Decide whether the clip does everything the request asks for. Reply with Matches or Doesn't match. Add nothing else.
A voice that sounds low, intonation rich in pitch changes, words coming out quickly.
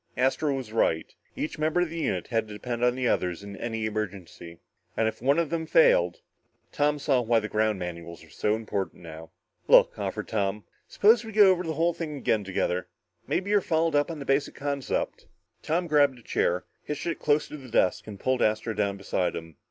Matches